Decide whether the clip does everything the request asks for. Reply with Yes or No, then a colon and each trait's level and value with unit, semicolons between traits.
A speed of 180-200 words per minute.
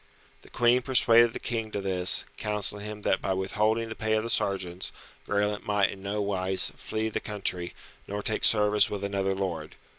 Yes: average, 185 wpm